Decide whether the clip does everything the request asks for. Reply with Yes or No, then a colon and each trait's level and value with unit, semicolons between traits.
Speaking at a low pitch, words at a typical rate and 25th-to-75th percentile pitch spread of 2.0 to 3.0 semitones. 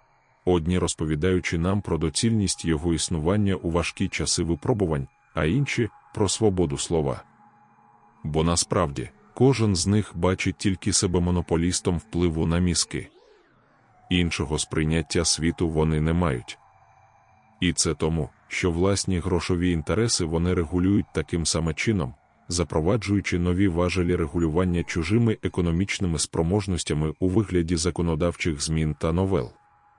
Yes: very low, 90 Hz; average, 120 wpm; narrow, 2.6 semitones